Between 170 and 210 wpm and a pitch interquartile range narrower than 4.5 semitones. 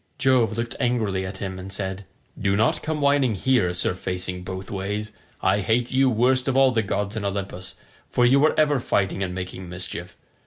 No: average, 195 wpm; average, 5.0 semitones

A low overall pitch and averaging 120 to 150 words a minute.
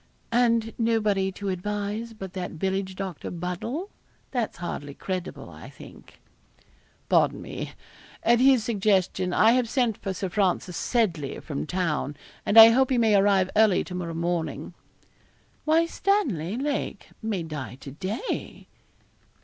No: high, 200 Hz; average, 140 wpm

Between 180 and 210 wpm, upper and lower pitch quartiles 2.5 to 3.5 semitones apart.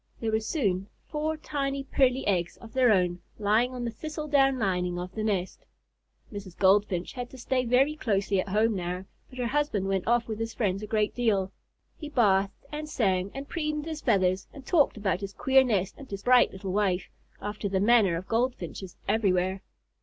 No: average, 195 wpm; average, 5.3 semitones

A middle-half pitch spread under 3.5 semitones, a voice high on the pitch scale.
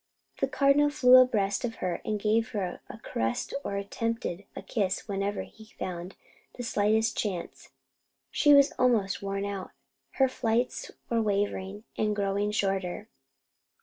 Yes: average, 2.8 semitones; high, 210 Hz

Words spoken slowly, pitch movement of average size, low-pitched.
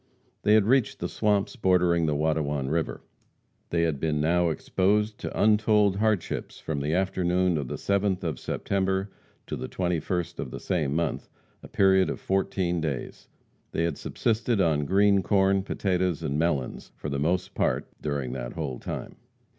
No: average, 165 wpm; average, 4.0 semitones; very low, 90 Hz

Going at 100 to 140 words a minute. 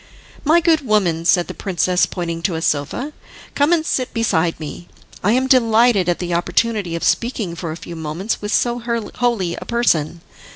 No: average, 180 wpm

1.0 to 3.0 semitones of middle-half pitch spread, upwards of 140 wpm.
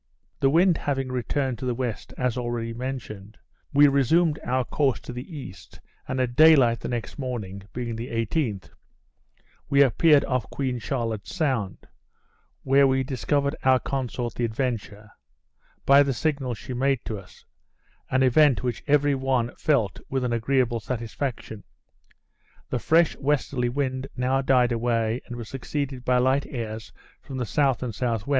Yes: average, 2.7 semitones; average, 160 wpm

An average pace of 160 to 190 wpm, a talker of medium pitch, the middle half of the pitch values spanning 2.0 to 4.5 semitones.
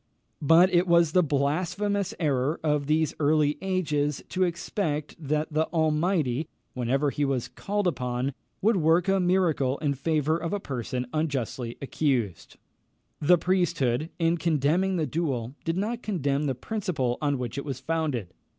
No: average, 150 wpm; medium, 155 Hz; average, 4.1 semitones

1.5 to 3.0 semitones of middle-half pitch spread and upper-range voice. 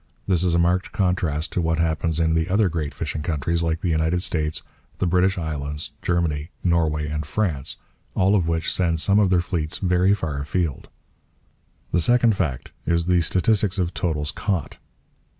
No: average, 2.7 semitones; very low, 85 Hz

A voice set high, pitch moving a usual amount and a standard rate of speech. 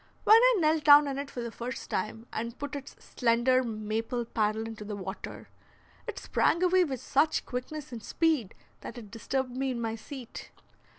Yes: very high, 250 Hz; average, 4.3 semitones; average, 185 wpm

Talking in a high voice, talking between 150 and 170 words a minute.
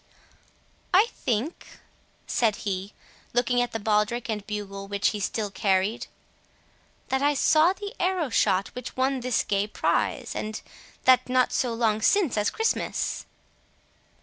No: high, 230 Hz; average, 140 wpm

